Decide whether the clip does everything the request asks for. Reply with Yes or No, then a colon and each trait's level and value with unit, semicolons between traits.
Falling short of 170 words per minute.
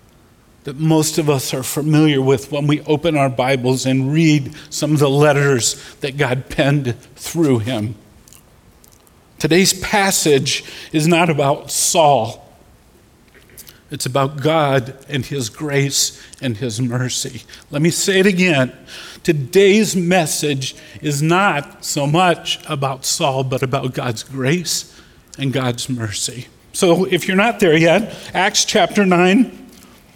Yes: slow, 135 wpm